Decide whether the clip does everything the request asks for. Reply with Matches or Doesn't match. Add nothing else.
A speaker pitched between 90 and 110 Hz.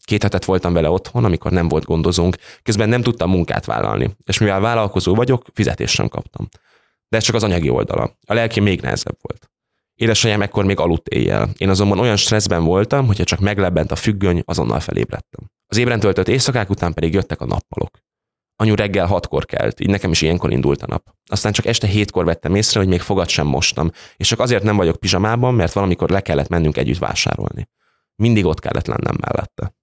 Matches